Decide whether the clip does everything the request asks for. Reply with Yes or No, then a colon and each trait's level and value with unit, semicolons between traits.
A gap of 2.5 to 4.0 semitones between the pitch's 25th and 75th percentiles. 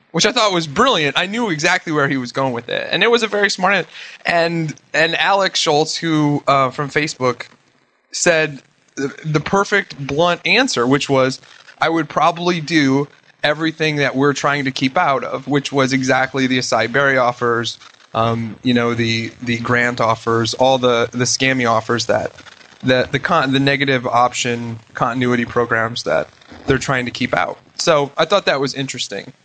No: average, 4.5 semitones